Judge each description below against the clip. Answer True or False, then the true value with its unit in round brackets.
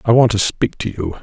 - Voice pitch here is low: True (105 Hz)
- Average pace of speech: False (295 wpm)